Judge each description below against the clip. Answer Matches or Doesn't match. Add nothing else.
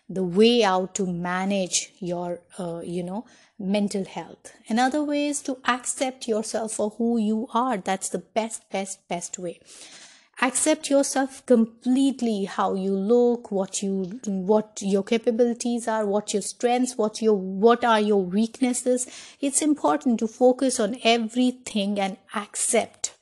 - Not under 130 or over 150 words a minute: Matches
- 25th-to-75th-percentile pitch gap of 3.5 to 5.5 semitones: Matches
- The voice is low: Doesn't match